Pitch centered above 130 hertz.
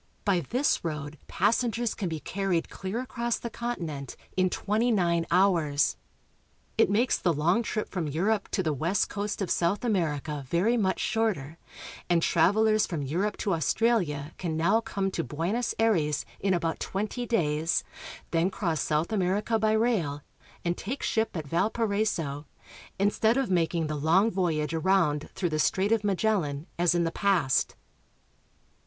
Yes: medium, 185 Hz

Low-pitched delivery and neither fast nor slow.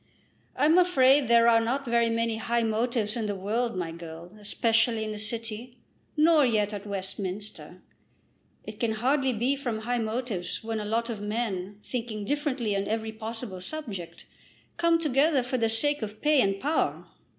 No: high, 230 Hz; average, 170 wpm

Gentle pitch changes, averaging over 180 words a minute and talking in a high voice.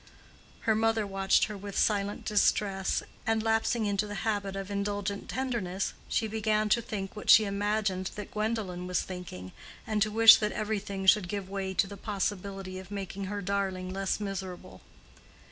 No: narrow, 1.8 semitones; average, 165 wpm; high, 200 Hz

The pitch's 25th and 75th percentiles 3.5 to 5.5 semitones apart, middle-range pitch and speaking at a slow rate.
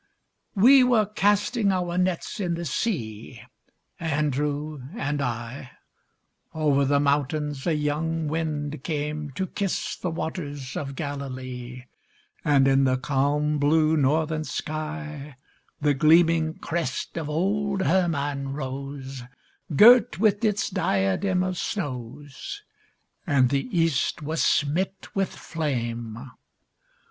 Yes: average, 3.8 semitones; medium, 150 Hz; slow, 115 wpm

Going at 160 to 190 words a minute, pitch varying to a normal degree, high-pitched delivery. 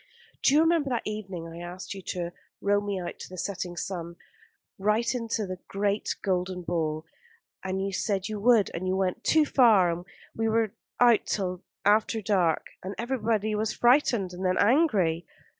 Yes: average, 180 wpm; average, 3.6 semitones; high, 195 Hz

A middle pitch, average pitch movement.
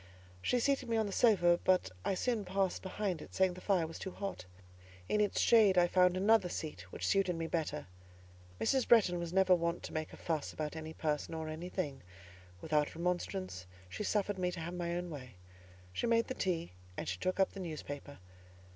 Yes: medium, 180 Hz; average, 3.5 semitones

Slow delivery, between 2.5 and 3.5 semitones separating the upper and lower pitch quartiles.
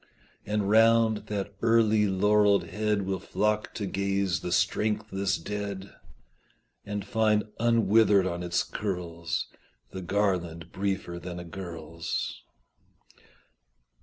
Yes: slow, 105 wpm; average, 3.0 semitones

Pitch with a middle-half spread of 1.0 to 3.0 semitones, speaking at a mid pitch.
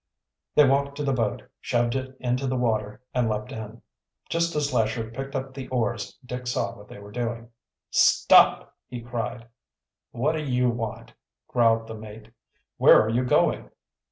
No: narrow, 2.6 semitones; low, 120 Hz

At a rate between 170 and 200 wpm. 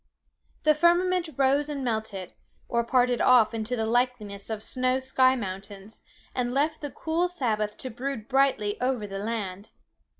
No: average, 155 wpm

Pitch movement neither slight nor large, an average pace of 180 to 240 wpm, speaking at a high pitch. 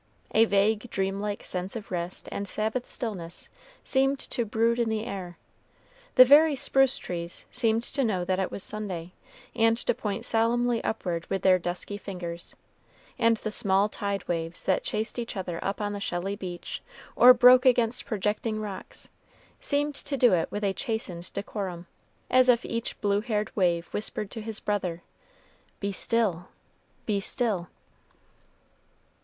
No: average, 3.7 semitones; average, 155 wpm; high, 210 Hz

